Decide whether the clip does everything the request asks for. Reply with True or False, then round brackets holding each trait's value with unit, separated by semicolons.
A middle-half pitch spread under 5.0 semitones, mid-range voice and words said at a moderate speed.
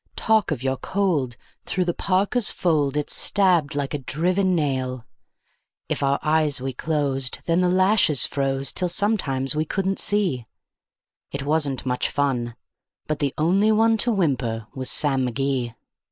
False (5.5 semitones; 150 Hz; 155 wpm)